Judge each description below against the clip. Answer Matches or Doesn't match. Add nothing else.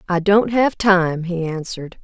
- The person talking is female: Matches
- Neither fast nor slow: Matches